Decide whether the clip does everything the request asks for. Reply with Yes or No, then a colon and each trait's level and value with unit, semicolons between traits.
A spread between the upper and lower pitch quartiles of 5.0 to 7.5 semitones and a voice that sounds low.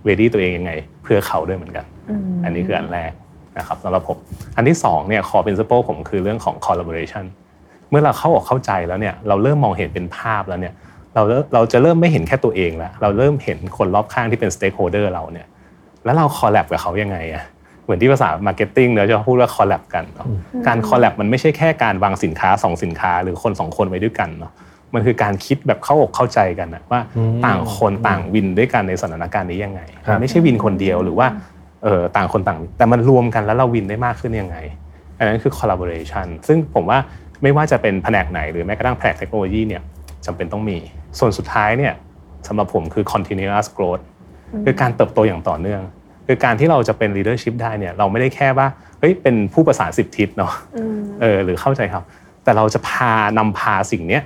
Yes: wide, 5.4 semitones; low, 105 Hz